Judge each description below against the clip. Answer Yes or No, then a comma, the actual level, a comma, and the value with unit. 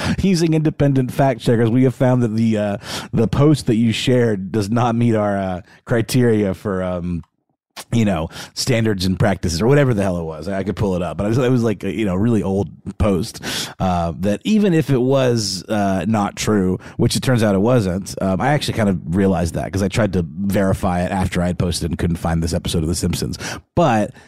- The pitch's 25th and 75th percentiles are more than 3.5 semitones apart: Yes, average, 4.5 semitones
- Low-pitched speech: Yes, low, 105 Hz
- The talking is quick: Yes, fast, 220 wpm